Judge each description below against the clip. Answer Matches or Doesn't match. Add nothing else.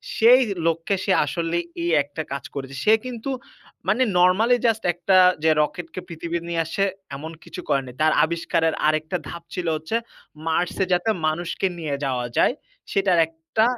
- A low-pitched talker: Doesn't match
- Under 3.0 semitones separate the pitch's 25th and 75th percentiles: Doesn't match